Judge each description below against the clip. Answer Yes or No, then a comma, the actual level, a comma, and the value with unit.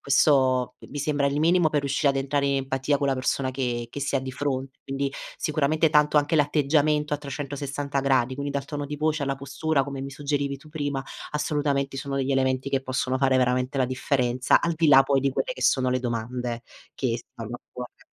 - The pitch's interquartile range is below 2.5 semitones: Yes, narrow, 1.8 semitones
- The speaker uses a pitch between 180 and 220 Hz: No, medium, 140 Hz